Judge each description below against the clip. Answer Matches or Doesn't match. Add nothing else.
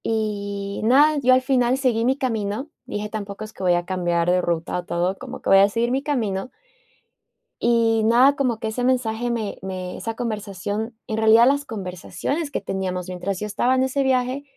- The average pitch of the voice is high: Matches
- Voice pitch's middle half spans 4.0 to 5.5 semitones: Matches